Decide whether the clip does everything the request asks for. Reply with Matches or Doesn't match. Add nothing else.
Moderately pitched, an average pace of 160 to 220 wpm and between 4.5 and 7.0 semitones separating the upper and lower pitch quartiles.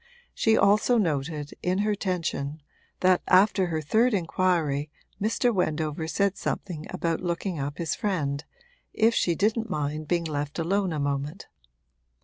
Doesn't match